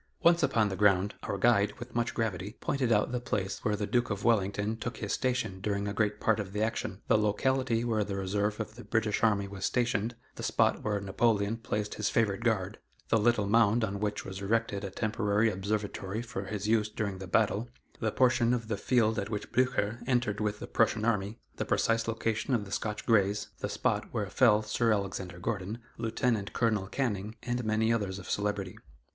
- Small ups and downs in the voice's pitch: Yes, narrow, 2.3 semitones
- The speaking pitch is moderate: No, low, 105 Hz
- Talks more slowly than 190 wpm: No, average, 200 wpm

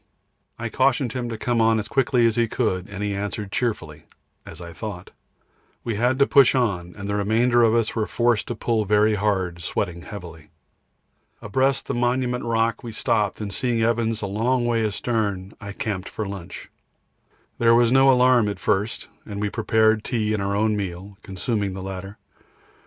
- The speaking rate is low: No, average, 185 wpm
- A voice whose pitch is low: Yes, low, 110 Hz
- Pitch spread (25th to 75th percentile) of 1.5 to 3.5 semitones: Yes, average, 2.9 semitones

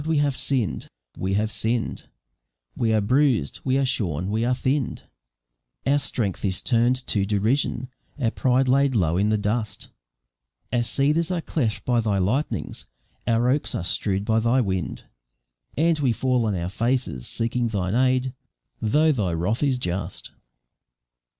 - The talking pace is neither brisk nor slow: Yes, average, 155 wpm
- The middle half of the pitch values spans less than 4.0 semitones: No, average, 4.4 semitones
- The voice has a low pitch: Yes, low, 115 Hz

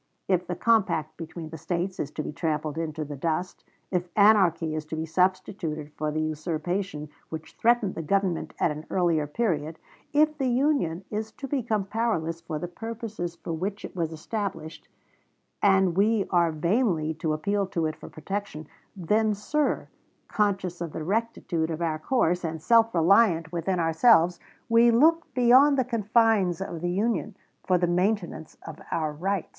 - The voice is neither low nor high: Yes, medium, 180 Hz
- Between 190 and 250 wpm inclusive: No, average, 170 wpm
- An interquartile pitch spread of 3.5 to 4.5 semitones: No, average, 5.0 semitones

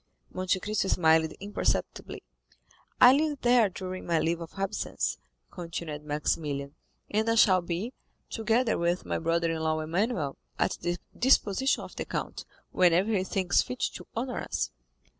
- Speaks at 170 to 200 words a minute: No, average, 150 wpm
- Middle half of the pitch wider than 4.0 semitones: Yes, average, 5.0 semitones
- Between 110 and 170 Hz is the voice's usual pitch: No, medium, 185 Hz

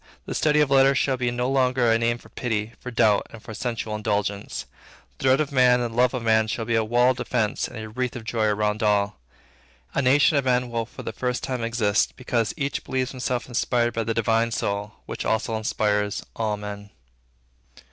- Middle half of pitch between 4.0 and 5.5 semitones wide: No, average, 2.7 semitones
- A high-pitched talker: No, low, 115 Hz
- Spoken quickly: Yes, fast, 215 wpm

